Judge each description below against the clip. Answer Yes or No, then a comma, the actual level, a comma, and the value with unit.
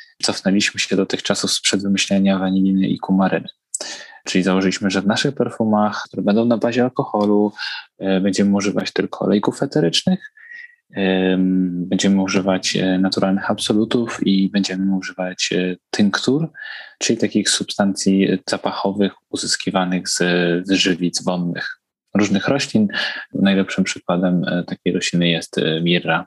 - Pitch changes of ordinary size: No, narrow, 2.1 semitones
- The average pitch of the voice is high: No, very low, 95 Hz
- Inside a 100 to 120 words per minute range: Yes, average, 115 wpm